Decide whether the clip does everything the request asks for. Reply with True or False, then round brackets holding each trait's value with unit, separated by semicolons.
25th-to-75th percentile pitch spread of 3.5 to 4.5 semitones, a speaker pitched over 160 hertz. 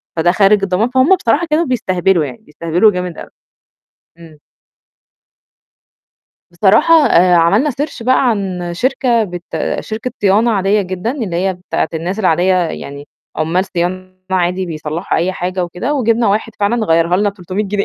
True (4.2 semitones; 190 Hz)